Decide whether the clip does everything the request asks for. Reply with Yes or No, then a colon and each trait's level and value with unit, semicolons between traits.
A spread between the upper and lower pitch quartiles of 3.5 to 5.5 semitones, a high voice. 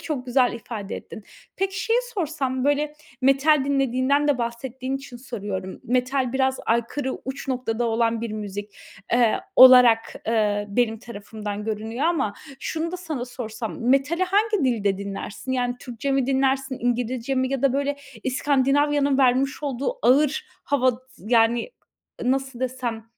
No: average, 2.9 semitones; very high, 255 Hz